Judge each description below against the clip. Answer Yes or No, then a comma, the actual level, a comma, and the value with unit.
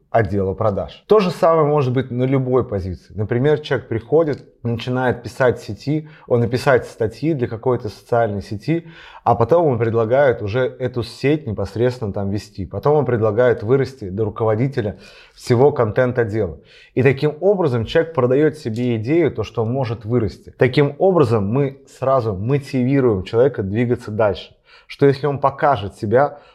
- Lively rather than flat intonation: No, average, 4.2 semitones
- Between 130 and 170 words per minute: Yes, average, 155 wpm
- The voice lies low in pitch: Yes, low, 125 Hz